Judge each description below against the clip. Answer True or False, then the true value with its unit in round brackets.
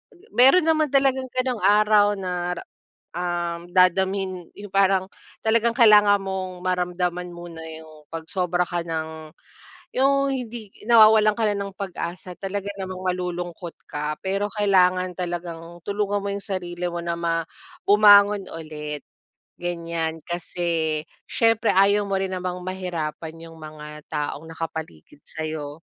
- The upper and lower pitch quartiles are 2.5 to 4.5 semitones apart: True (3.2 semitones)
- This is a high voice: False (180 Hz)